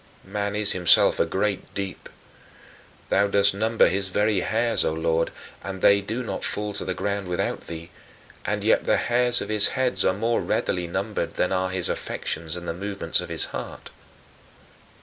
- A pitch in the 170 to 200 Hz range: No, low, 100 Hz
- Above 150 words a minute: Yes, average, 180 wpm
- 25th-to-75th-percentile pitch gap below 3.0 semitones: Yes, narrow, 2.5 semitones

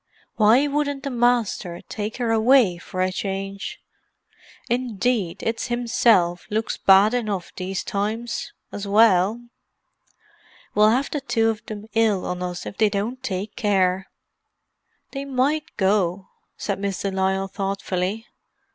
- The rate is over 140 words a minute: No, slow, 135 wpm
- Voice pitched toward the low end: No, high, 210 Hz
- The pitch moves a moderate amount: Yes, average, 3.8 semitones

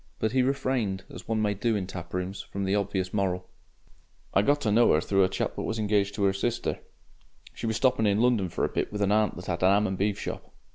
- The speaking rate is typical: No, fast, 250 wpm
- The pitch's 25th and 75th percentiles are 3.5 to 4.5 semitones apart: No, average, 2.7 semitones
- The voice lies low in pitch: Yes, low, 100 Hz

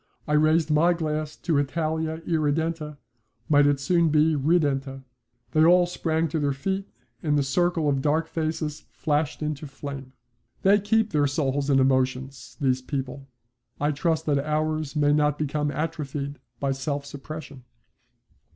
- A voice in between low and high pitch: Yes, medium, 150 Hz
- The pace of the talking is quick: No, average, 150 wpm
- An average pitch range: No, narrow, 2.2 semitones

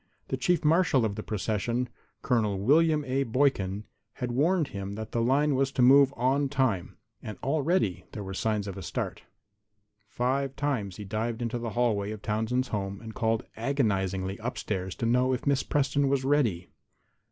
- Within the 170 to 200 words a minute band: Yes, average, 175 wpm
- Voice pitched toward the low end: Yes, low, 120 Hz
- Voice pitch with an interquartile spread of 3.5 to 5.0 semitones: Yes, average, 4.7 semitones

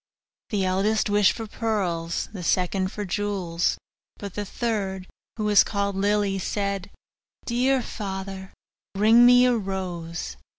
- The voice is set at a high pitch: Yes, high, 200 Hz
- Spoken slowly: Yes, slow, 130 wpm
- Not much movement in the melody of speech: Yes, narrow, 2.1 semitones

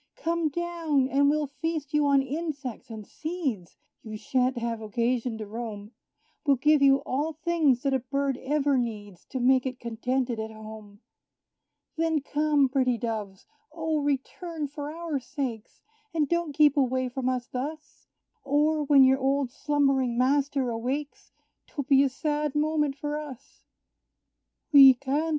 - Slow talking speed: No, average, 150 wpm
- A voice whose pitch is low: No, very high, 275 Hz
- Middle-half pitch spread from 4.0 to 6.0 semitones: No, average, 3.2 semitones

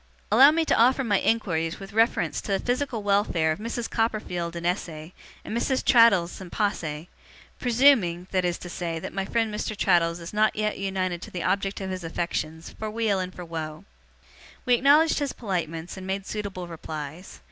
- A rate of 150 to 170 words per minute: No, average, 190 wpm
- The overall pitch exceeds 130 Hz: Yes, high, 190 Hz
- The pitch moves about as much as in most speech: Yes, average, 4.7 semitones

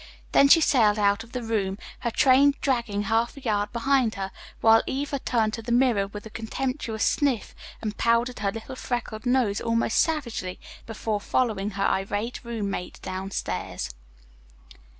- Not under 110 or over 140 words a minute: No, average, 160 wpm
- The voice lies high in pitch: Yes, high, 225 Hz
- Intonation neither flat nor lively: Yes, average, 3.5 semitones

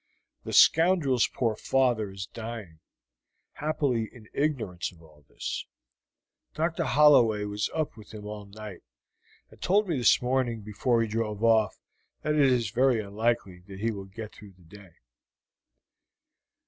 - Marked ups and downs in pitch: No, average, 4.3 semitones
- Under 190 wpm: Yes, average, 150 wpm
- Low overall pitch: Yes, low, 115 Hz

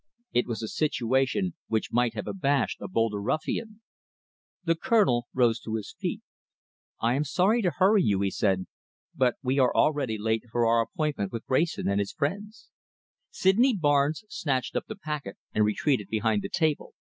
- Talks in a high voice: No, low, 130 Hz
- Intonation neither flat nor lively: No, wide, 6.9 semitones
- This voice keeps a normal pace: Yes, average, 170 wpm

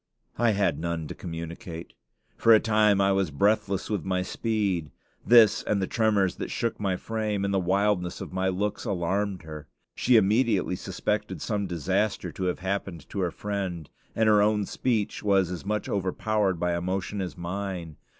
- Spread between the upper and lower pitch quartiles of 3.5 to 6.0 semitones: No, average, 2.8 semitones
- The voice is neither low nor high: No, low, 100 Hz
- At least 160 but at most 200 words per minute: Yes, average, 175 wpm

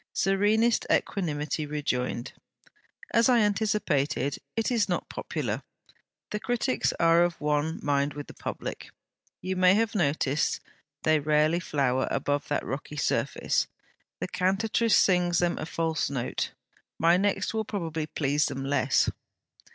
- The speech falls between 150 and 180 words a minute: No, slow, 135 wpm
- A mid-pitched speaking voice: Yes, medium, 165 Hz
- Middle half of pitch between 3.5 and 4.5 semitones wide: No, wide, 5.5 semitones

